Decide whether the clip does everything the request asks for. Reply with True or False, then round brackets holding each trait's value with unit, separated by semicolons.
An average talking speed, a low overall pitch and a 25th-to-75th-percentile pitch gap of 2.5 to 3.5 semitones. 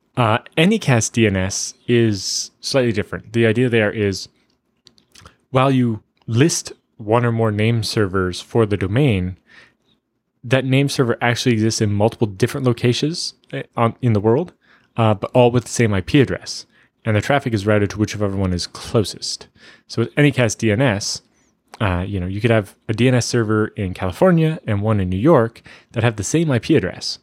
True (170 wpm; 115 Hz; 3.1 semitones)